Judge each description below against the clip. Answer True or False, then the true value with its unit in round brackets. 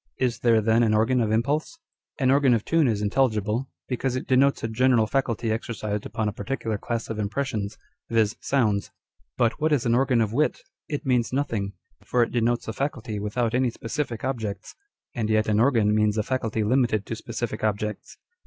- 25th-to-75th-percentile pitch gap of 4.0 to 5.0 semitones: False (3.2 semitones)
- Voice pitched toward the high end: False (115 Hz)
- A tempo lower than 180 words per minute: False (190 wpm)